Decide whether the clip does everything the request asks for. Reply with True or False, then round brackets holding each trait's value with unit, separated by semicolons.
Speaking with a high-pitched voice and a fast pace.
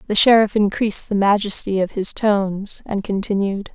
False (205 Hz; 160 wpm)